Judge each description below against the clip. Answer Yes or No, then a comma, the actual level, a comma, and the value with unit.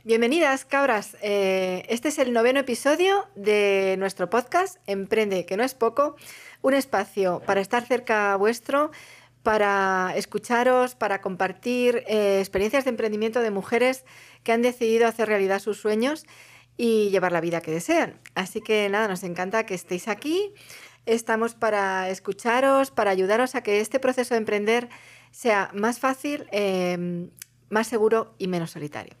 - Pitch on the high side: Yes, high, 220 Hz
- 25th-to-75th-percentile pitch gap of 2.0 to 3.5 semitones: No, average, 4.1 semitones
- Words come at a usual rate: Yes, average, 150 wpm